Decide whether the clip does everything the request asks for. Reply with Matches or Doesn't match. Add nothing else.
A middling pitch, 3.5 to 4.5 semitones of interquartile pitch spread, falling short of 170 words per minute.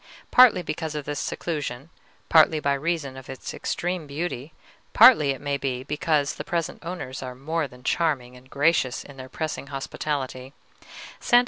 Matches